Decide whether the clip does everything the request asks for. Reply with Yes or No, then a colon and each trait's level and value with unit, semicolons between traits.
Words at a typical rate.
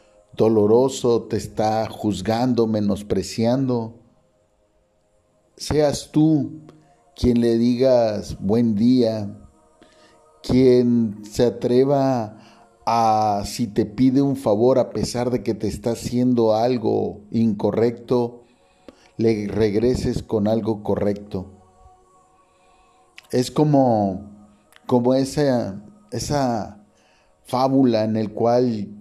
No: slow, 90 wpm